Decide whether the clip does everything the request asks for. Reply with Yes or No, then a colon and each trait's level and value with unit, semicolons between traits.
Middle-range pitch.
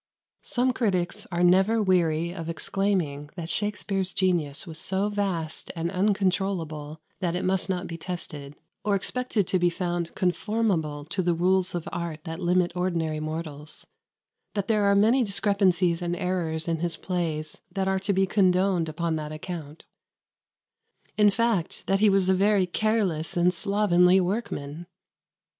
Yes: medium, 180 Hz